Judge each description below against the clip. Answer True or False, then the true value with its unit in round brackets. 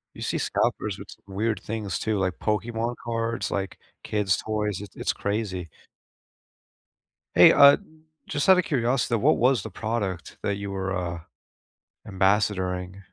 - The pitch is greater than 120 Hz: False (105 Hz)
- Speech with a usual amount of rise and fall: True (3.2 semitones)